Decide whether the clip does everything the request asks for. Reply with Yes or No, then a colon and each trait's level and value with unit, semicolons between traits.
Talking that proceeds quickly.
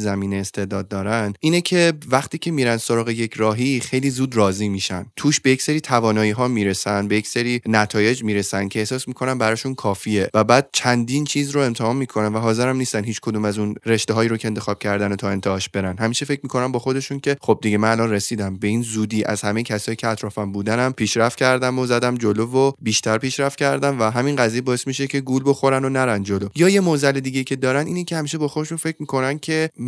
Yes: fast, 215 wpm